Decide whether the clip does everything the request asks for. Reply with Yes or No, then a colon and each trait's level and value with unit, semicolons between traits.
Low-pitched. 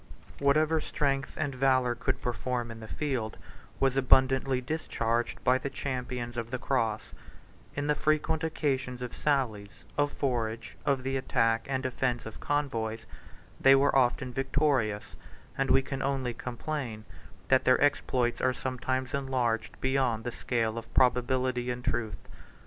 Yes: low, 130 Hz